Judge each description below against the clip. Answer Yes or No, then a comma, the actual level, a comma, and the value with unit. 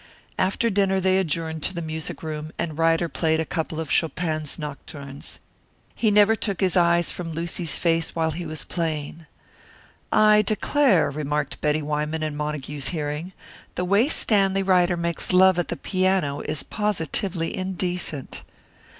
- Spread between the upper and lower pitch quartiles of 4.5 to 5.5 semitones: No, average, 3.5 semitones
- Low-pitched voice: No, medium, 165 Hz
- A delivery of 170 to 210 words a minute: No, average, 150 wpm